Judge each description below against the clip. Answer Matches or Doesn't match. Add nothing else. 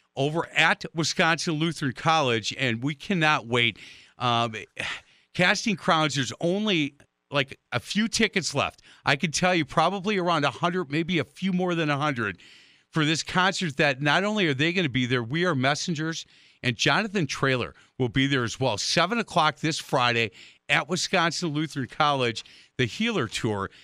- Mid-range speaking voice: Matches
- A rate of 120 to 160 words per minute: Doesn't match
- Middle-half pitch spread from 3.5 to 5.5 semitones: Matches